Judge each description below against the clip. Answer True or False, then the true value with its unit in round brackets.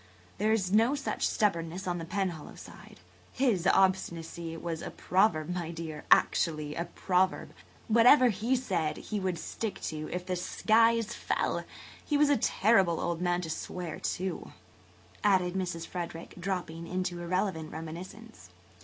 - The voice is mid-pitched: True (180 Hz)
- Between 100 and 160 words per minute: True (145 wpm)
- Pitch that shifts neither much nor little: True (4.0 semitones)